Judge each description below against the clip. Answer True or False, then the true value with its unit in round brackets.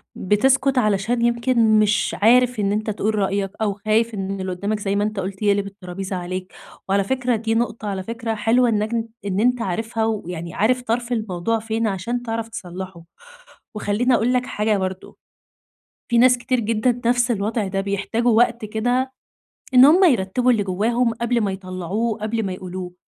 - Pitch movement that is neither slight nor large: True (3.3 semitones)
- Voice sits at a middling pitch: False (215 Hz)